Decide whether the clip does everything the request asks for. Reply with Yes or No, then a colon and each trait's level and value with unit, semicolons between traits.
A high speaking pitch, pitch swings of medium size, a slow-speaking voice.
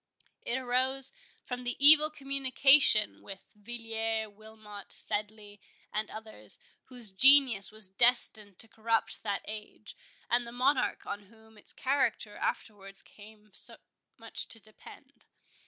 Yes: high, 220 Hz; average, 3.2 semitones; slow, 125 wpm